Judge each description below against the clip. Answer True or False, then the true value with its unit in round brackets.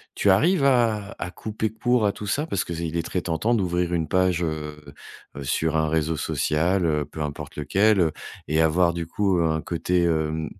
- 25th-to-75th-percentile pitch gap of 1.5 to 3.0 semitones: False (4.1 semitones)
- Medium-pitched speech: False (85 Hz)